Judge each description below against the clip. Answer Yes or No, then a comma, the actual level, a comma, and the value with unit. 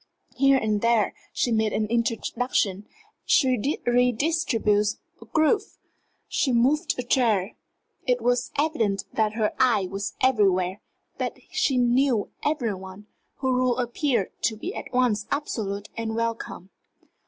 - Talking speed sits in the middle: No, slow, 130 wpm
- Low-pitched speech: No, high, 235 Hz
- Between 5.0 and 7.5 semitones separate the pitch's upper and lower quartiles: No, average, 3.5 semitones